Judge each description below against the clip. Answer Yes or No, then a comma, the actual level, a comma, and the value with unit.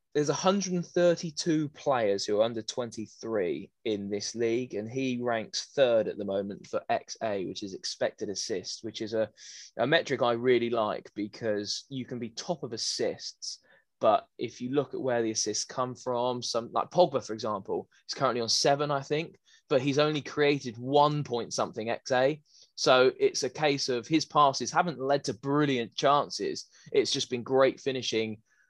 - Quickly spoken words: No, average, 175 wpm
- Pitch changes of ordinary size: Yes, average, 4.4 semitones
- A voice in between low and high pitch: No, low, 130 Hz